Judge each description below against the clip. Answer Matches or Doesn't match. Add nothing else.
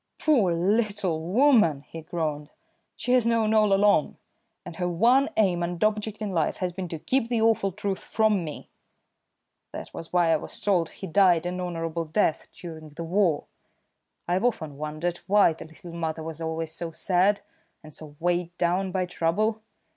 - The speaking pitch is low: Doesn't match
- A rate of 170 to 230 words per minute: Matches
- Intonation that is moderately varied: Matches